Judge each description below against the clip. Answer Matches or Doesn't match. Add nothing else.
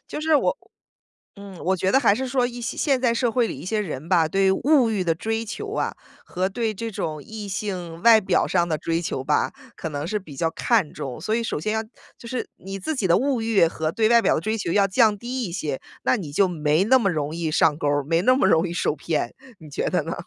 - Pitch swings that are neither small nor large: Doesn't match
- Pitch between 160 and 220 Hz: Matches